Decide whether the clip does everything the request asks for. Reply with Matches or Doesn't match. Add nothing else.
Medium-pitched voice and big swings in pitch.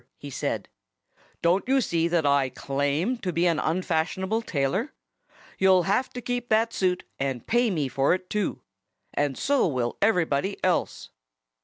Matches